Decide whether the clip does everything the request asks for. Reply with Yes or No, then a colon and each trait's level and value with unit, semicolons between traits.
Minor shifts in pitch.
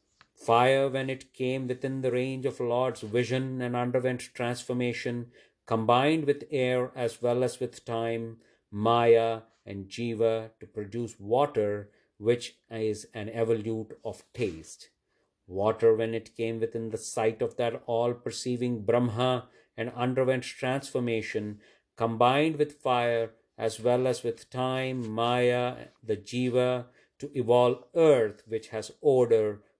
Yes: narrow, 1.9 semitones